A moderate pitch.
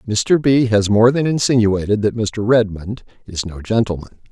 No: low, 110 Hz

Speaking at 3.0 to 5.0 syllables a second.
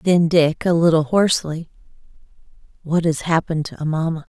No: 5.6 syllables/s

